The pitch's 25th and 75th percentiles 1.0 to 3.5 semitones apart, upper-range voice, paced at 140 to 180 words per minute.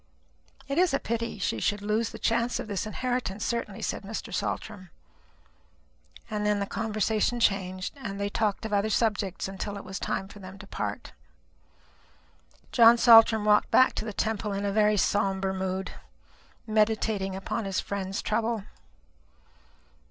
Yes: narrow, 2.4 semitones; high, 210 Hz; average, 155 wpm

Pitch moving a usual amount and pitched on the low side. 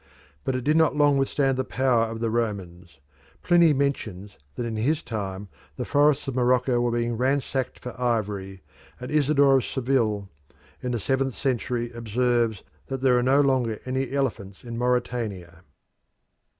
Yes: average, 3.3 semitones; low, 125 Hz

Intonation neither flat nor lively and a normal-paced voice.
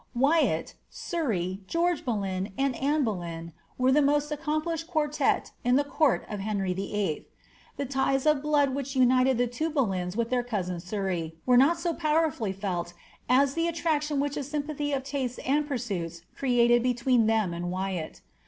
No: wide, 6.9 semitones; average, 165 wpm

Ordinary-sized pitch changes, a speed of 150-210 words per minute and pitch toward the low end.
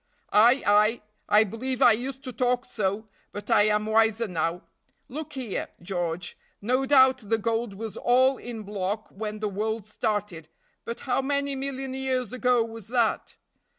No: average, 3.5 semitones; average, 160 wpm; high, 225 Hz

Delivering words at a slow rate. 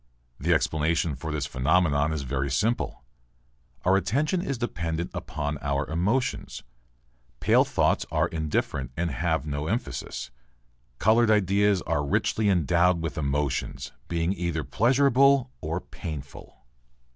Yes: slow, 120 wpm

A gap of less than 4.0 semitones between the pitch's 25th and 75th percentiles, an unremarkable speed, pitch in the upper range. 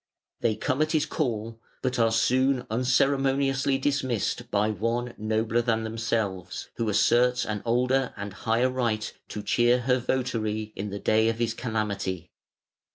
No: average, 2.9 semitones; average, 150 wpm; low, 115 Hz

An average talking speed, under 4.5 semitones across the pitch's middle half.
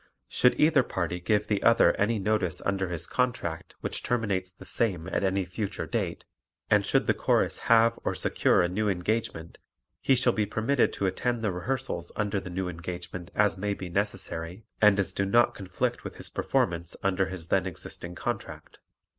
Yes: average, 180 wpm; average, 3.7 semitones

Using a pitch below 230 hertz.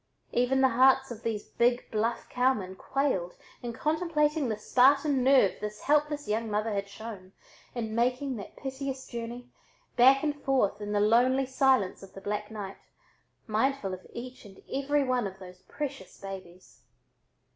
No: high, 240 Hz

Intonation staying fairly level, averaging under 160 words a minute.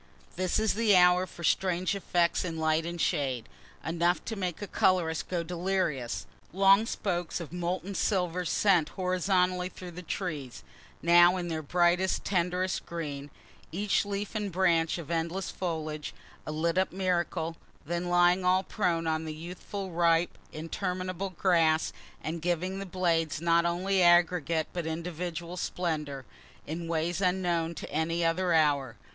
Yes: narrow, 2.1 semitones; average, 150 wpm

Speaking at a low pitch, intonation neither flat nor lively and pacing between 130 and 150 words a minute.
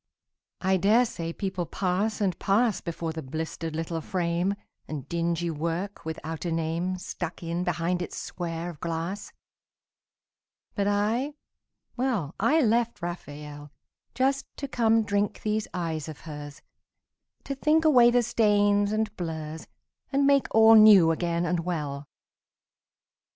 No: medium, 180 Hz; average, 4.7 semitones; slow, 135 wpm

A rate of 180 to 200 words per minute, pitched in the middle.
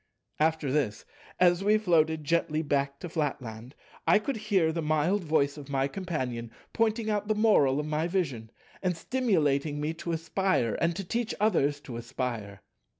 No: average, 160 wpm; medium, 160 Hz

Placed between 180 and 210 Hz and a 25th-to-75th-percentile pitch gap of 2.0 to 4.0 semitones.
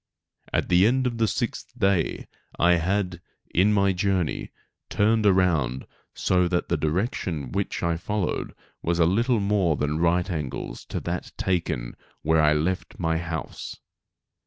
No: very low, 90 Hz; average, 3.5 semitones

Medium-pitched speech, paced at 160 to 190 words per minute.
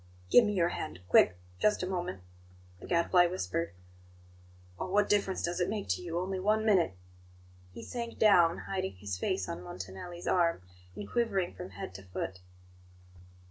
Yes: medium, 175 Hz; average, 165 wpm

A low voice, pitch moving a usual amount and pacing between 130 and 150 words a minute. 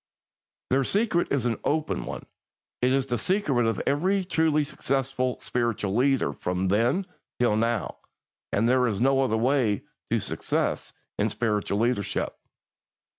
Yes: low, 125 Hz; average, 3.8 semitones; average, 140 wpm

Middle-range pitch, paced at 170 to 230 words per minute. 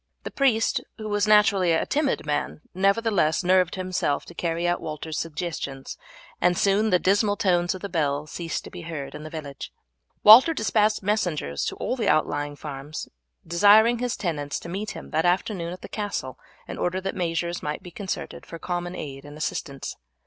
Yes: medium, 175 Hz; average, 185 wpm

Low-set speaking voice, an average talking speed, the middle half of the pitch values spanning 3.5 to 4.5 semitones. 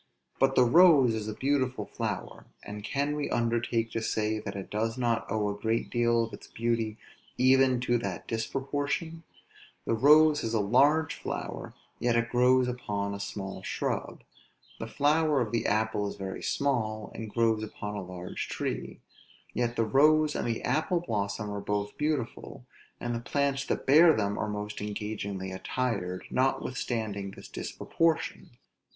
Yes: low, 115 Hz; average, 160 wpm; average, 4.2 semitones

